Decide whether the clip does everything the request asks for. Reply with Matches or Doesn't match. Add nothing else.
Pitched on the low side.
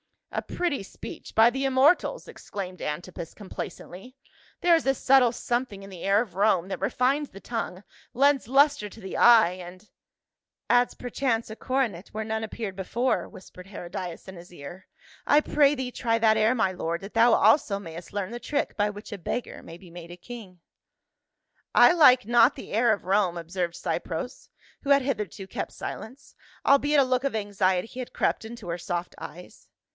Doesn't match